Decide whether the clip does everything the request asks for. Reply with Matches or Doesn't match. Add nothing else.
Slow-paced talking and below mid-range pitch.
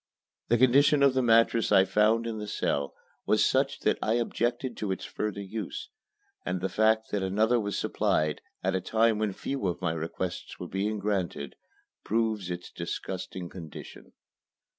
Doesn't match